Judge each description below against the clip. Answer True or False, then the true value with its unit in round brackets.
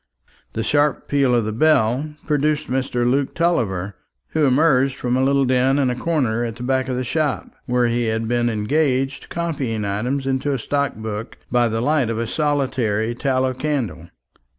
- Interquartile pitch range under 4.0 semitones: True (3.4 semitones)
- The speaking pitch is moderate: False (130 Hz)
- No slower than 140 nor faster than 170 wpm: False (180 wpm)